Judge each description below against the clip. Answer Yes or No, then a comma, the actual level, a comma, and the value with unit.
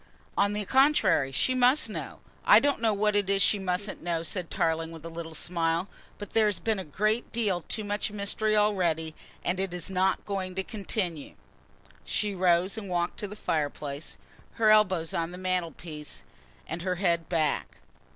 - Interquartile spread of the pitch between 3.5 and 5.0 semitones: Yes, average, 3.9 semitones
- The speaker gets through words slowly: No, average, 180 wpm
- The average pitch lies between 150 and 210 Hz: Yes, medium, 185 Hz